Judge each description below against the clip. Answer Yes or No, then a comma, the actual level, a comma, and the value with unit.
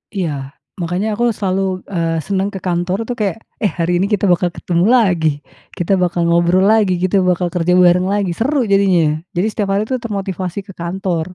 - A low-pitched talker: No, medium, 185 Hz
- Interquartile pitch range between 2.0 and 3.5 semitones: Yes, narrow, 2.4 semitones